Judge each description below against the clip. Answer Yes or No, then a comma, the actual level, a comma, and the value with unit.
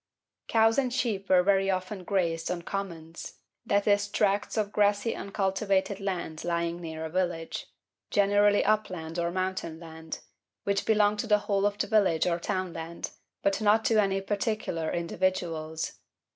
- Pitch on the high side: Yes, high, 195 Hz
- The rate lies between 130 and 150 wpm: Yes, average, 145 wpm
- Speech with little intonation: No, average, 3.3 semitones